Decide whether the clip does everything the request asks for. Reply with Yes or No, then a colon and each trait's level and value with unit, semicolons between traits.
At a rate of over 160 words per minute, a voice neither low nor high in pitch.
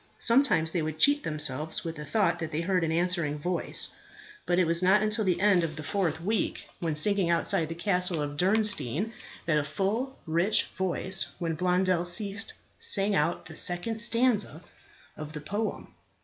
Yes: average, 175 wpm; medium, 175 Hz